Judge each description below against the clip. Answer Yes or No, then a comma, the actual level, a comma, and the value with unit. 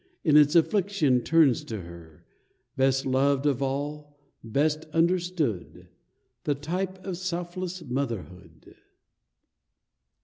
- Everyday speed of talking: No, slow, 105 wpm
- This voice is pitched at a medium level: Yes, medium, 145 Hz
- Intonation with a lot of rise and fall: No, average, 4.9 semitones